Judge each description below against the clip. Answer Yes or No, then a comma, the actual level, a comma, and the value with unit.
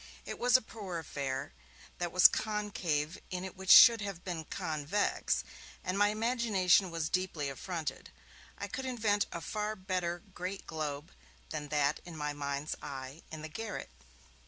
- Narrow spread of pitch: No, average, 5.3 semitones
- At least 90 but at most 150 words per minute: No, average, 160 wpm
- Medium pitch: Yes, medium, 175 Hz